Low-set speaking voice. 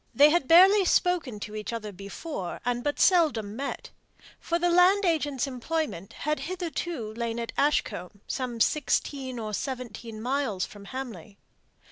No: very high, 260 Hz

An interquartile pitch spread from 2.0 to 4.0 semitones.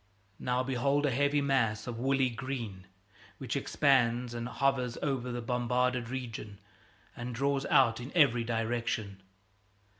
Yes: narrow, 2.6 semitones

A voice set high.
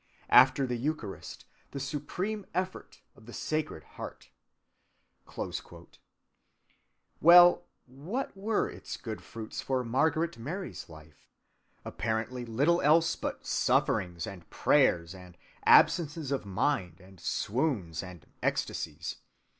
No: low, 130 Hz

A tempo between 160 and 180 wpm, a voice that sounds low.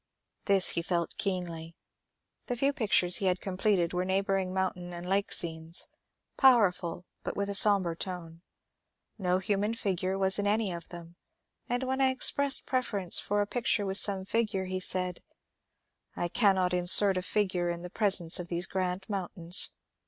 No: average, 175 wpm; high, 190 Hz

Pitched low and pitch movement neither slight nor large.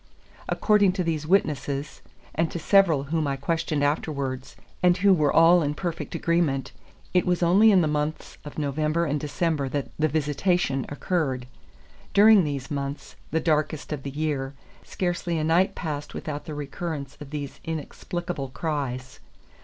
No: medium, 155 Hz; average, 3.3 semitones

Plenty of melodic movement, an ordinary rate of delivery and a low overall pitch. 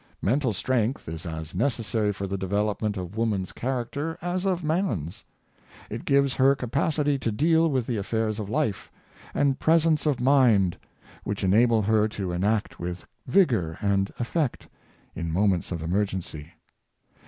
Yes: wide, 6.2 semitones; average, 150 wpm; low, 110 Hz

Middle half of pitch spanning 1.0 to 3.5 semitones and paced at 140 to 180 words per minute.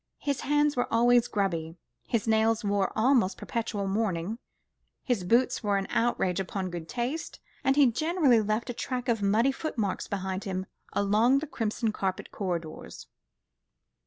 No: average, 4.1 semitones; average, 155 wpm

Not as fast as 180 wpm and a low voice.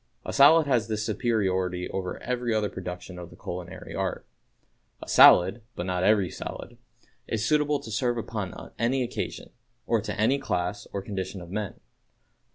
Yes: average, 165 wpm; low, 105 Hz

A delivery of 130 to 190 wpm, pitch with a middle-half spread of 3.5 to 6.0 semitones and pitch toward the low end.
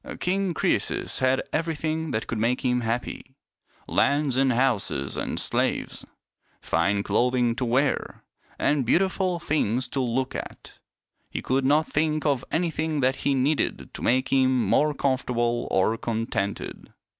Yes: average, 145 wpm; average, 4.0 semitones; low, 130 Hz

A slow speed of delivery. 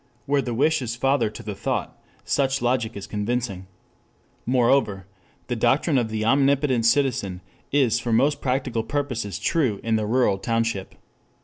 No: average, 150 wpm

